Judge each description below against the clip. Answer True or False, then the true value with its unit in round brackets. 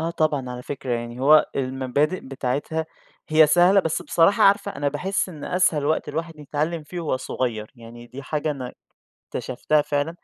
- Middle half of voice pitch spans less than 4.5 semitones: True (4.0 semitones)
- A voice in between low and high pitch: True (150 Hz)